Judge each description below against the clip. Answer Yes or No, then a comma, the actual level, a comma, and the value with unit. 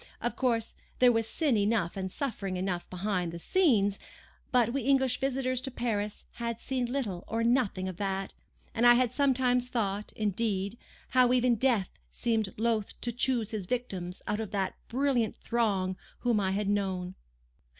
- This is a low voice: No, high, 225 Hz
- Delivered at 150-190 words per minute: Yes, average, 160 wpm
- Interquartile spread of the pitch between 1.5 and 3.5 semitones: No, average, 4.1 semitones